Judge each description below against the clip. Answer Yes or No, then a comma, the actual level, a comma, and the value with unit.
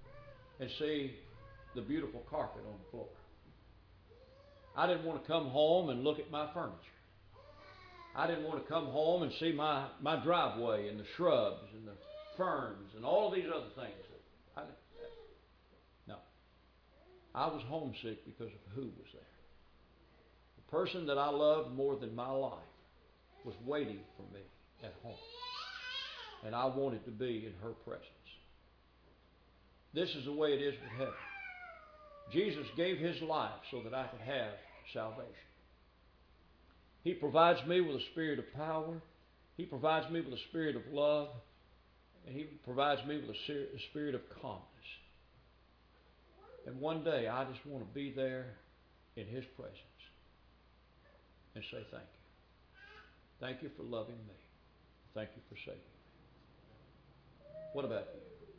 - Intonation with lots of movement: Yes, wide, 8.1 semitones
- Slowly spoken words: No, average, 155 wpm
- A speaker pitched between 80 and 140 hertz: Yes, low, 135 Hz